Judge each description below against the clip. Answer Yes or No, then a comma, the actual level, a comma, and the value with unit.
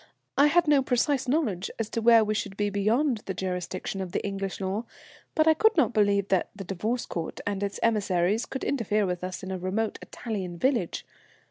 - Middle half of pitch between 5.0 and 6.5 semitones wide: No, average, 4.1 semitones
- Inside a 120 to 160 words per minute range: No, fast, 205 wpm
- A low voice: No, high, 205 Hz